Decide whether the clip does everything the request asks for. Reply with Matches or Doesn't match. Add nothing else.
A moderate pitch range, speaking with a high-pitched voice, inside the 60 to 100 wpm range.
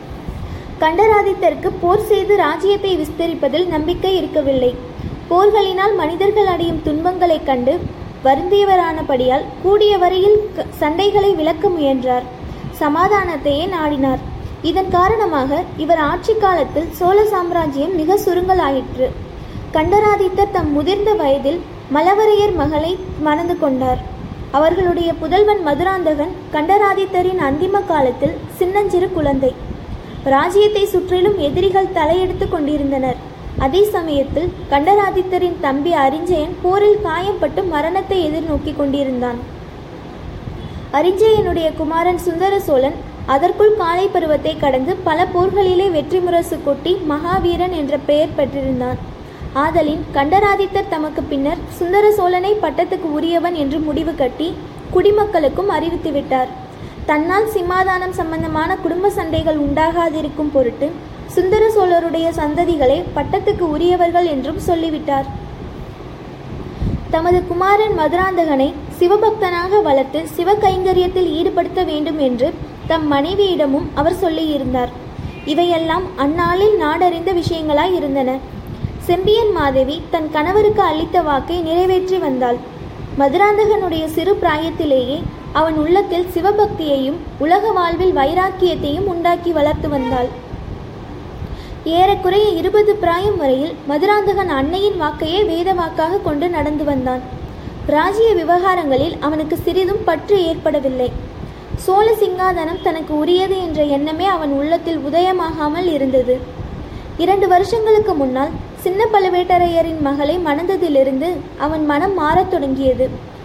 Matches